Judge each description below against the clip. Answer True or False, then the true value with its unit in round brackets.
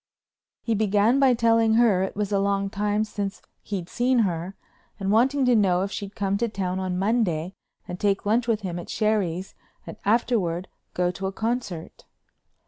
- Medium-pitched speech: False (200 Hz)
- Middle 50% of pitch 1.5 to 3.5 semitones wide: True (3.2 semitones)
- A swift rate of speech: False (180 wpm)